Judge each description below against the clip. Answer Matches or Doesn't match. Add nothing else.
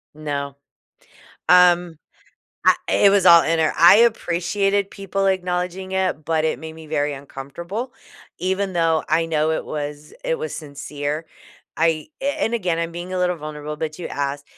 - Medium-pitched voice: Matches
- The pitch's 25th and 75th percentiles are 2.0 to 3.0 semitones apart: Doesn't match